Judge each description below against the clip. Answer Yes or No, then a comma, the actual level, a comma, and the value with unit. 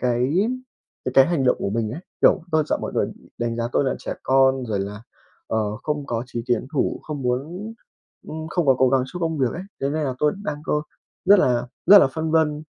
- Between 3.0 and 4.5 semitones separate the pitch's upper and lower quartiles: Yes, average, 4.2 semitones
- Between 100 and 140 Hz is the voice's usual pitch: Yes, low, 135 Hz